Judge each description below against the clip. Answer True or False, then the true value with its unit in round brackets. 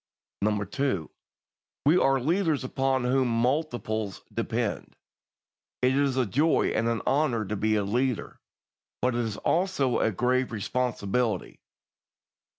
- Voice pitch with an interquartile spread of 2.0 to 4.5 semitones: True (3.3 semitones)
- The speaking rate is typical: False (125 wpm)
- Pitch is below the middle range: True (125 Hz)